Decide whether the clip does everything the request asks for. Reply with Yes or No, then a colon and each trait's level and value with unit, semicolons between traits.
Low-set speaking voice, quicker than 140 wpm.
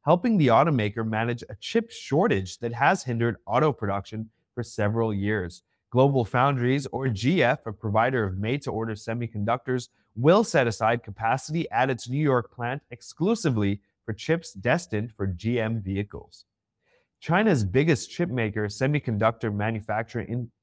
No: low, 115 Hz; slow, 135 wpm